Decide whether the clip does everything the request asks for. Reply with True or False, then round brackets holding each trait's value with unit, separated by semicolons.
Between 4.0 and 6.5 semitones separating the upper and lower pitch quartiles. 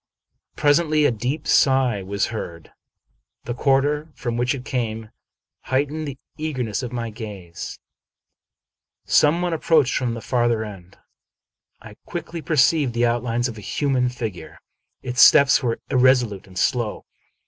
True (4.3 semitones)